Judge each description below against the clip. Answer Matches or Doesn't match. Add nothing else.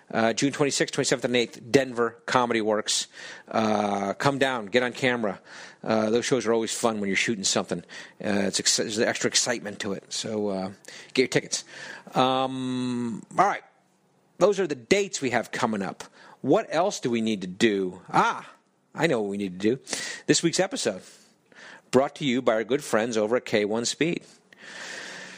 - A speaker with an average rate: Matches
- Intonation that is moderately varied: Matches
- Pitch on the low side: Matches